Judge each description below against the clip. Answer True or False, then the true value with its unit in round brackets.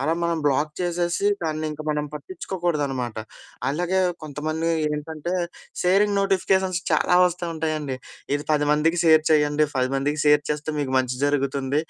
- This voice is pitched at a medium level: True (155 Hz)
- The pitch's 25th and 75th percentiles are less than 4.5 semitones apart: True (2.9 semitones)